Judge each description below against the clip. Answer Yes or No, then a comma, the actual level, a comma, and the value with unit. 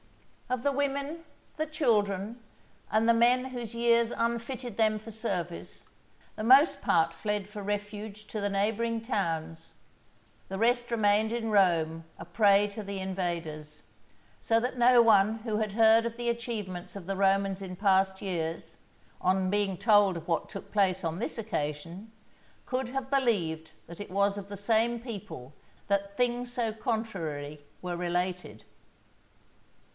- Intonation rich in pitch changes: No, average, 3.8 semitones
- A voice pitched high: Yes, high, 205 Hz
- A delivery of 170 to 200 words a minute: No, average, 150 wpm